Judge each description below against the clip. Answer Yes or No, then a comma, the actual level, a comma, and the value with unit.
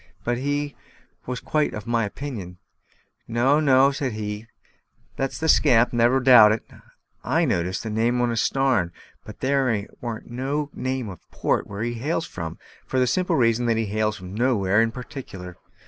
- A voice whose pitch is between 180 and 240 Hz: No, low, 120 Hz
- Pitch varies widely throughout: No, average, 3.7 semitones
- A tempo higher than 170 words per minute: Yes, average, 185 wpm